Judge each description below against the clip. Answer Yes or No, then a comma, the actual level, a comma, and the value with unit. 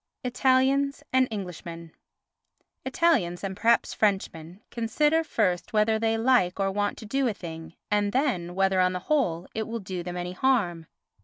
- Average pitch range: No, wide, 6.0 semitones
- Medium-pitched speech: No, high, 205 Hz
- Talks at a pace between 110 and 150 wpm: No, average, 160 wpm